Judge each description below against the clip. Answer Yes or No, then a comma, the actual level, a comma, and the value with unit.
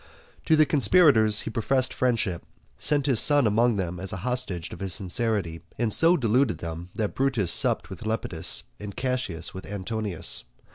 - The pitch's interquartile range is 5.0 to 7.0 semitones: Yes, wide, 5.5 semitones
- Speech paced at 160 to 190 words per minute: Yes, average, 165 wpm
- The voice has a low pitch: Yes, low, 110 Hz